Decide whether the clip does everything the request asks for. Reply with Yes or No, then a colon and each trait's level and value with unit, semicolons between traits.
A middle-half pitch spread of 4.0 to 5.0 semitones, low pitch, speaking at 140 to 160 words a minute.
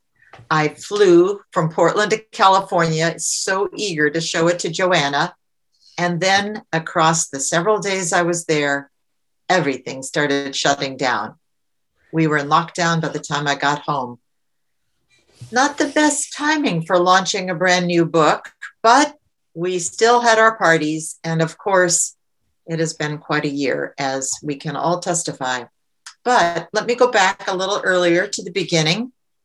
No: average, 4.4 semitones; medium, 170 Hz; average, 155 wpm